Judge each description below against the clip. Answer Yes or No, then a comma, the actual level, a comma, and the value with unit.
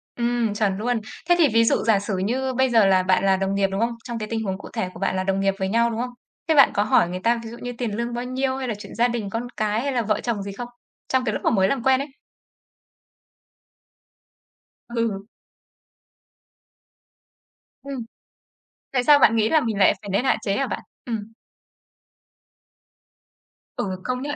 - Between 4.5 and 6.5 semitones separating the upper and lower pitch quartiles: No, average, 3.7 semitones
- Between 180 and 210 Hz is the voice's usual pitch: No, high, 230 Hz